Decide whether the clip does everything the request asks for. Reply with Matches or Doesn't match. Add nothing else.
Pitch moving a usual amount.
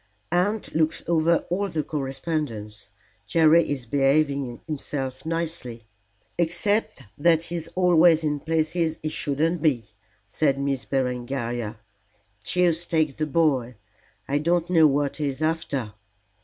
Matches